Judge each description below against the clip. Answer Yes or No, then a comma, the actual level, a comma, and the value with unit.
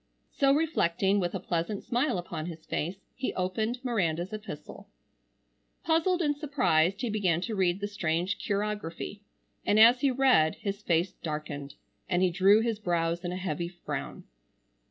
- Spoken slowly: No, average, 155 wpm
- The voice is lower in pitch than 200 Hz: Yes, high, 190 Hz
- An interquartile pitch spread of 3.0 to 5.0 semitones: Yes, average, 4.7 semitones